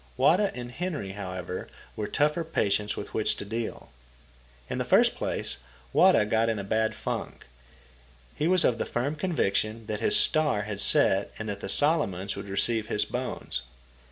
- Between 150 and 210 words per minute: Yes, average, 170 wpm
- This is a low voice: Yes, low, 110 Hz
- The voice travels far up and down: Yes, wide, 6.6 semitones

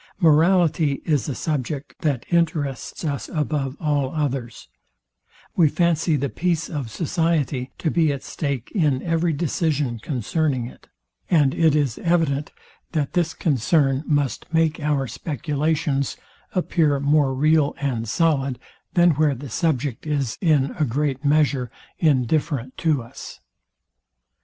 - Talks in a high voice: No, medium, 145 Hz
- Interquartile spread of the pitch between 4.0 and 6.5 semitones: No, average, 2.9 semitones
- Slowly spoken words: Yes, slow, 130 wpm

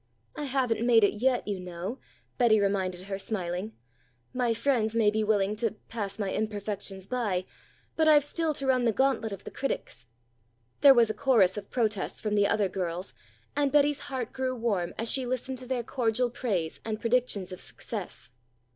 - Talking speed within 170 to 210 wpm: Yes, average, 180 wpm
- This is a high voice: Yes, high, 220 Hz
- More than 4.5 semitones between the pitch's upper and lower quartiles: No, average, 4.2 semitones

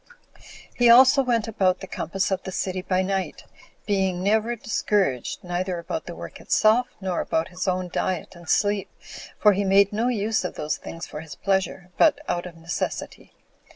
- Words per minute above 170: Yes, average, 180 wpm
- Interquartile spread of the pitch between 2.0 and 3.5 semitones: Yes, average, 2.8 semitones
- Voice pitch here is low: No, high, 190 Hz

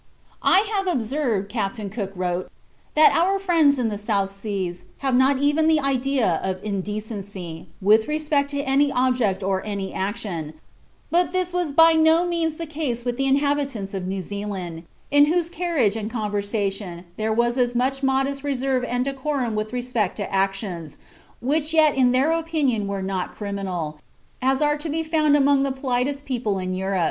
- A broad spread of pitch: Yes, wide, 6.4 semitones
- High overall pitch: Yes, very high, 250 Hz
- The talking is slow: No, average, 175 wpm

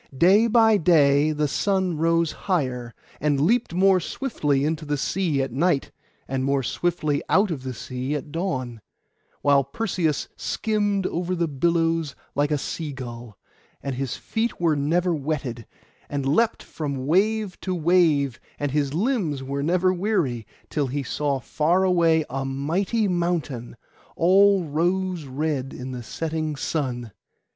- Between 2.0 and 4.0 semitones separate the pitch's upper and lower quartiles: No, average, 4.8 semitones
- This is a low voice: No, medium, 155 Hz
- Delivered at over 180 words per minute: No, average, 150 wpm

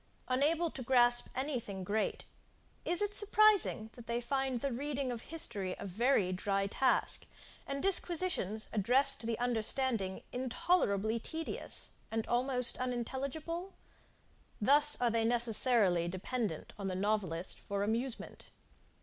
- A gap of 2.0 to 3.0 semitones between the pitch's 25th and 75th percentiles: No, average, 4.5 semitones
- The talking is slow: Yes, slow, 130 wpm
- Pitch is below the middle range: No, high, 240 Hz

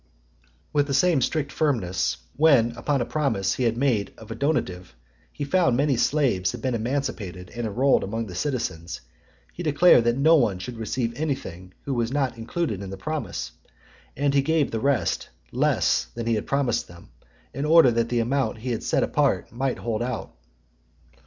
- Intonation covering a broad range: No, average, 4.3 semitones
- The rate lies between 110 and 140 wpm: No, average, 185 wpm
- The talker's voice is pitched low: Yes, low, 120 Hz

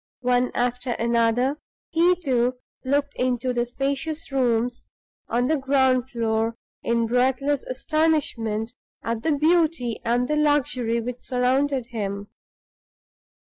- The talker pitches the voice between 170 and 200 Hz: No, very high, 250 Hz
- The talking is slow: Yes, slow, 115 wpm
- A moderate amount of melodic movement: Yes, average, 3.1 semitones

